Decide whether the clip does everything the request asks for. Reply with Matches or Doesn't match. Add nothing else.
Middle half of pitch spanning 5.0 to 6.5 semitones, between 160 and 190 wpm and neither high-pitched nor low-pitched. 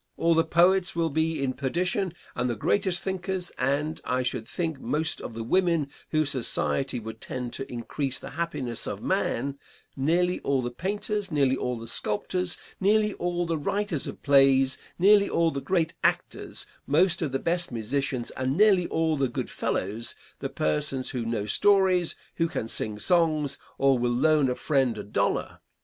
Matches